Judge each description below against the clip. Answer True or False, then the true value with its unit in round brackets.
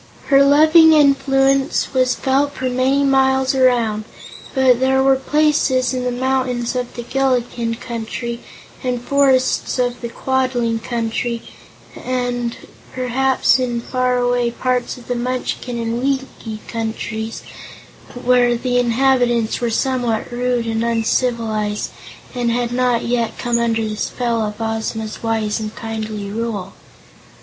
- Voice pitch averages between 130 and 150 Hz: False (245 Hz)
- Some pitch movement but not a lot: False (2.2 semitones)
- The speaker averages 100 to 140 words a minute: True (135 wpm)